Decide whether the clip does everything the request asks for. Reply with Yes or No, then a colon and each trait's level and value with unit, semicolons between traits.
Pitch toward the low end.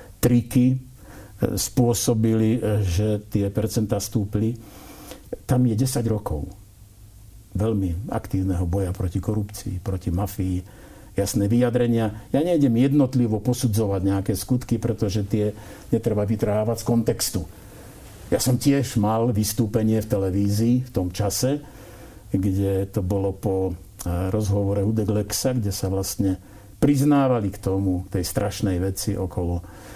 Yes: low, 105 Hz